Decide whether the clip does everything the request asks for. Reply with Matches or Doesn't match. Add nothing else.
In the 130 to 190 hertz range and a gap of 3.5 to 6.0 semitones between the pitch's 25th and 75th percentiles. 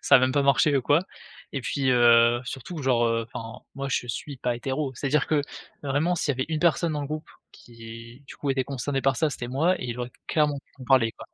Doesn't match